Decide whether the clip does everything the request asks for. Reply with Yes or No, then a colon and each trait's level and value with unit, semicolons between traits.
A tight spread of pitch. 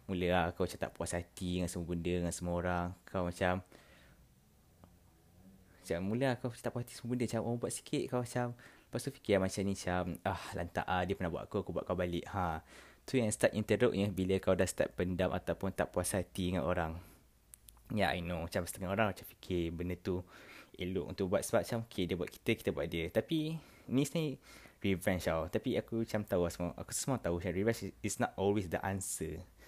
No: average, 3.8 semitones